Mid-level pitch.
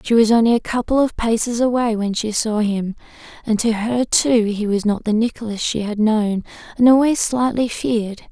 No: high, 225 Hz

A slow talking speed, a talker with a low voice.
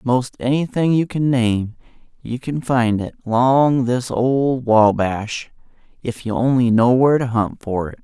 No: average, 165 wpm; low, 125 Hz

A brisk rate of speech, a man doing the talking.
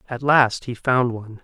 Yes: fast, 210 wpm; male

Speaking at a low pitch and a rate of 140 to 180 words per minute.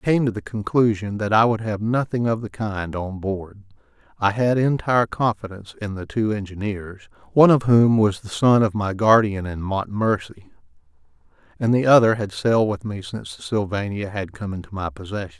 No: low, 105 Hz; average, 190 wpm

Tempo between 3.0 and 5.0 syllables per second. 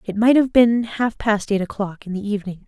No: 5.5 syllables/s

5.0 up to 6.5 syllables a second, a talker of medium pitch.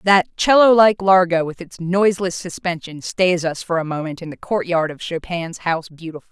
Yes: 5.2 syllables/s; medium, 175 Hz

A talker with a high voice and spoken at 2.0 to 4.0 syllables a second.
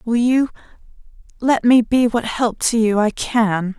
Yes: high, 230 Hz; 3.9 syllables/s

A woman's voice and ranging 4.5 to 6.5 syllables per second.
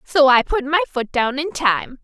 No: female; 4.3 syllables/s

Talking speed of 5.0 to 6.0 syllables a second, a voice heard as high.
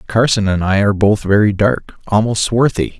No: 5.2 syllables/s; low, 105 Hz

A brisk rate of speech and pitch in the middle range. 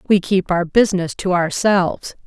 No: average, 160 wpm; medium, 180 Hz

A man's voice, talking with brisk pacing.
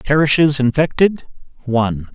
No: male; slow, 85 wpm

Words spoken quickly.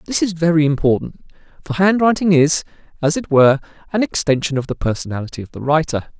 No: average, 175 wpm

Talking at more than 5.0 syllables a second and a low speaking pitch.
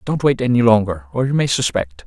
Yes: 5.8 syllables/s; low, 115 Hz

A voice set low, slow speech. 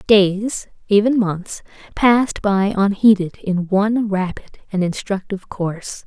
No: high, 200 Hz; slow, 120 wpm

